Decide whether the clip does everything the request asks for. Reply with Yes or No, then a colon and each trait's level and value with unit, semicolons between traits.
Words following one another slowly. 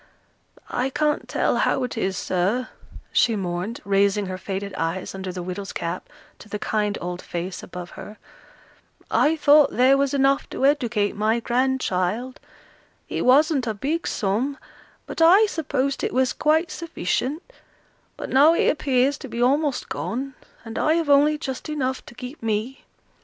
No: average, 160 wpm